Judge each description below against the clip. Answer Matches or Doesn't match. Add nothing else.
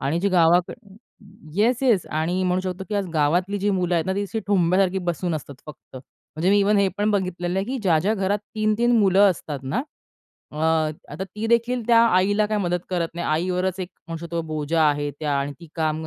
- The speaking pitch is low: Doesn't match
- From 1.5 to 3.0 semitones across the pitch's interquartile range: Doesn't match